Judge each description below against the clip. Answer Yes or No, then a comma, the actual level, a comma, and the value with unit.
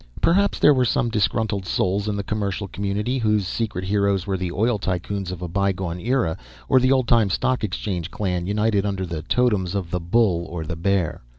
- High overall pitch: No, low, 100 Hz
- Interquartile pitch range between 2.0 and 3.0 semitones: No, average, 3.4 semitones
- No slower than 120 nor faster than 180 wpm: No, fast, 205 wpm